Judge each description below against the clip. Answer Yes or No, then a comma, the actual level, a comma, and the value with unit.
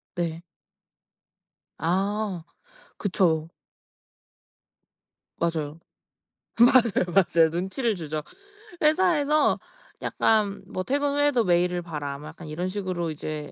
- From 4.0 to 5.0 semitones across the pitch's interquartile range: No, wide, 5.4 semitones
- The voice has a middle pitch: Yes, medium, 180 Hz